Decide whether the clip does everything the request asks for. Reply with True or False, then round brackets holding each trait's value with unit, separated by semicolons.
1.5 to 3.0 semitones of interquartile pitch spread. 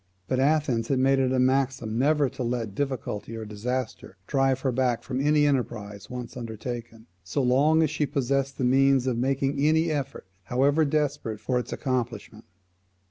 True (2.7 semitones)